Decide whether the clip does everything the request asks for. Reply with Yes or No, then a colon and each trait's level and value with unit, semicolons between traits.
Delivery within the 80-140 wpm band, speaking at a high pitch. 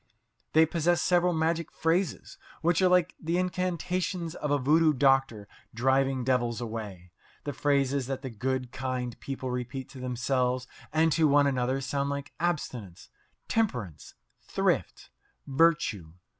No: slow, 135 wpm; low, 135 Hz